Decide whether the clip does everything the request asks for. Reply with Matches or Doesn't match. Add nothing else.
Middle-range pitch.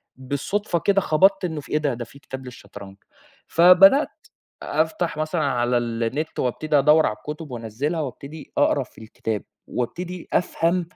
Matches